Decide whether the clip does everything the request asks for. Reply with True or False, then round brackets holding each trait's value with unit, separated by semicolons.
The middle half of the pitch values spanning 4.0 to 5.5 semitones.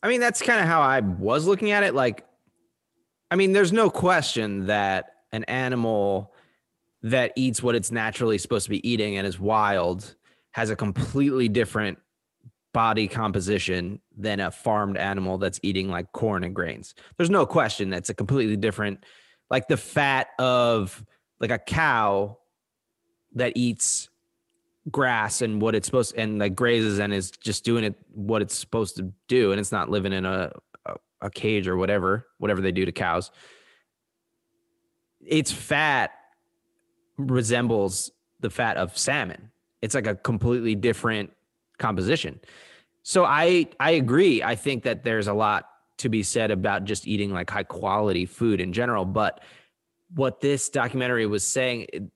True (4.7 semitones)